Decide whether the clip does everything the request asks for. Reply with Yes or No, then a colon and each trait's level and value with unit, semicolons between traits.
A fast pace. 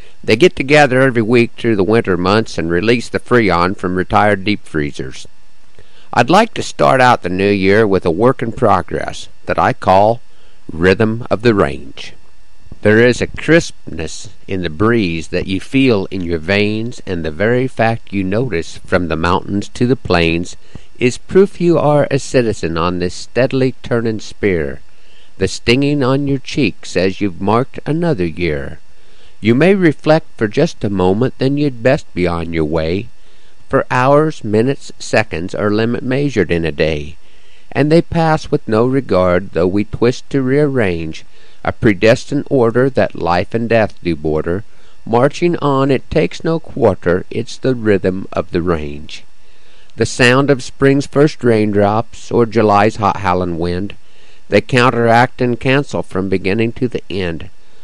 No: average, 165 wpm